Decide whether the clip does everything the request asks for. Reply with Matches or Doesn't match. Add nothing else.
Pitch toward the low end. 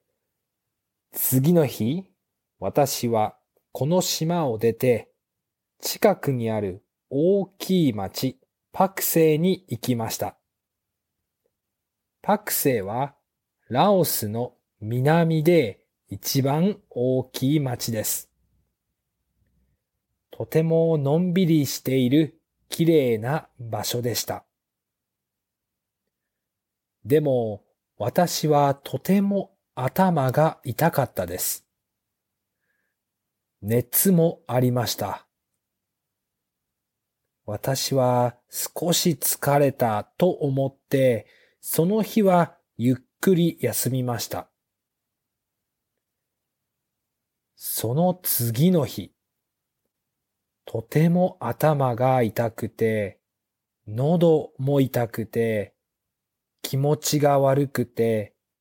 Matches